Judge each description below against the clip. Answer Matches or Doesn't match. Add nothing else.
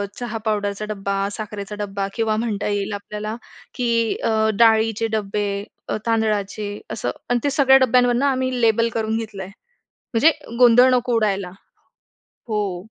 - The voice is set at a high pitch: Matches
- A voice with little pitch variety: Matches